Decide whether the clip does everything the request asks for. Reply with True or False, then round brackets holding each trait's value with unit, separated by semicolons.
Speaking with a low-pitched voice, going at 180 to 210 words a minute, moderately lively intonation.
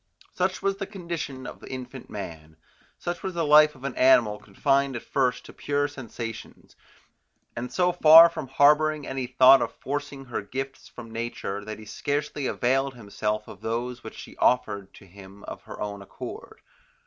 False (130 Hz; 170 wpm; 4.5 semitones)